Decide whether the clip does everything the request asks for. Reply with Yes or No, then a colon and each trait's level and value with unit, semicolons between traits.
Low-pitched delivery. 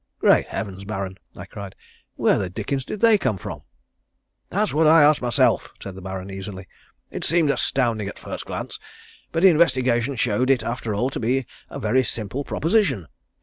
Yes: low, 120 Hz